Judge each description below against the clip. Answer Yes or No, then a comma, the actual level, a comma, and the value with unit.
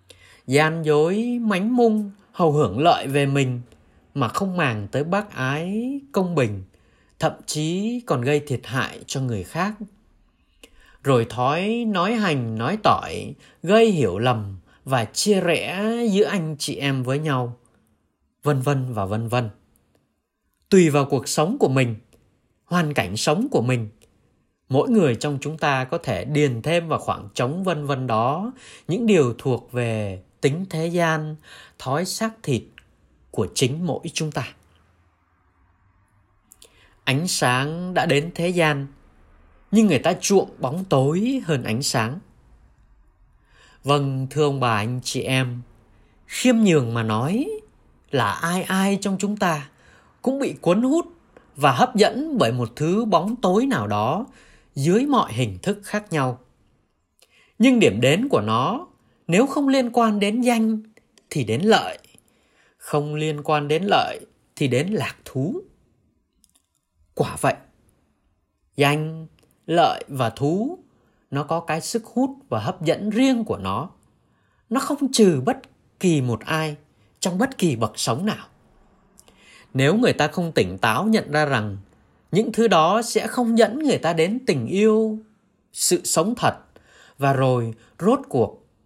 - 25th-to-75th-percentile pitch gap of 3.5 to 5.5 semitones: No, wide, 8.7 semitones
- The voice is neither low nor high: Yes, medium, 150 Hz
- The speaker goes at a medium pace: No, slow, 150 wpm